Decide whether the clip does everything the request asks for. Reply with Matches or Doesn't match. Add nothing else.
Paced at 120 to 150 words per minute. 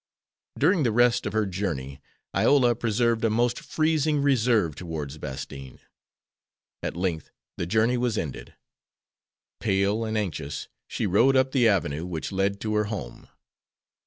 Matches